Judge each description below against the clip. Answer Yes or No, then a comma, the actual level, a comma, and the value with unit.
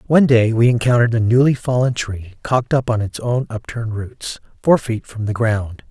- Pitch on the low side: Yes, low, 115 Hz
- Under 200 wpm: No, fast, 205 wpm